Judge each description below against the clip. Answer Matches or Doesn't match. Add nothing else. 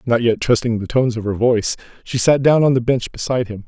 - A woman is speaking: Doesn't match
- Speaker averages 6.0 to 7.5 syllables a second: Matches